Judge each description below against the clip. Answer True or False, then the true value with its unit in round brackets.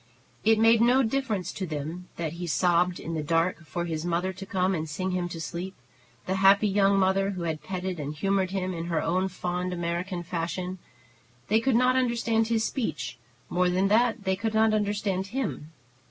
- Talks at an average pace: True (195 wpm)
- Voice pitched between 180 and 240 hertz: True (185 Hz)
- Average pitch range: True (3.3 semitones)